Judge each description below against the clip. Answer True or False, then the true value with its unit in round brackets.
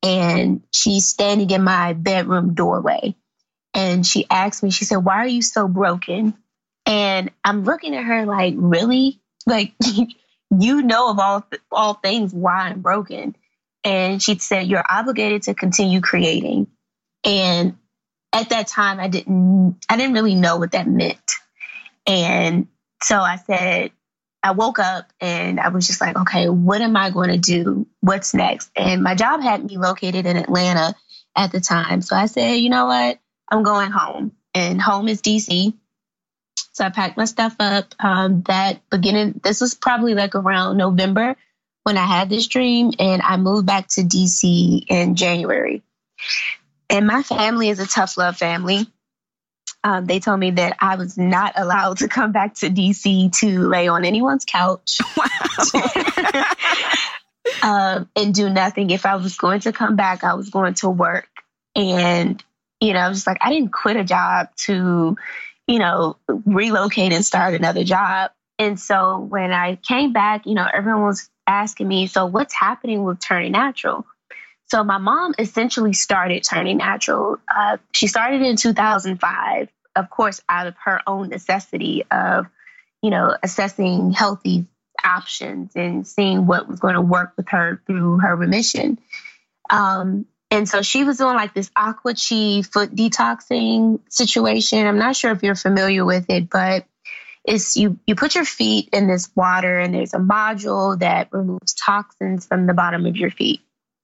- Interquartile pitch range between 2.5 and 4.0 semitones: True (2.8 semitones)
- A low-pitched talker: False (195 Hz)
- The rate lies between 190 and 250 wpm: False (170 wpm)